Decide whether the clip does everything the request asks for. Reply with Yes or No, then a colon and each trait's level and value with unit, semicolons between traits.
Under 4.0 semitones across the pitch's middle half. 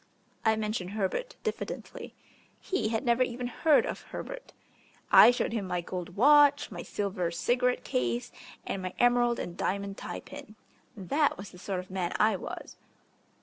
No: average, 5.1 semitones